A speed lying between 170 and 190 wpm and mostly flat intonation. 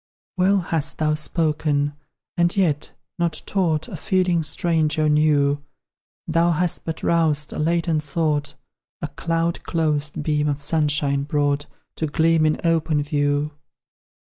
No: slow, 135 wpm; narrow, 2.1 semitones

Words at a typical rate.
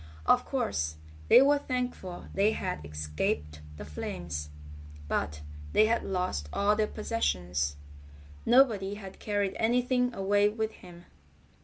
No: slow, 125 wpm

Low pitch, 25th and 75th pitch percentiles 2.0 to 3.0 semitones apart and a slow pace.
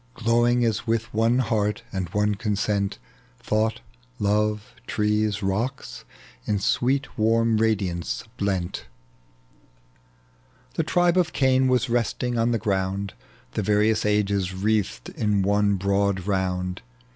Yes: low, 105 Hz; narrow, 2.6 semitones; slow, 120 wpm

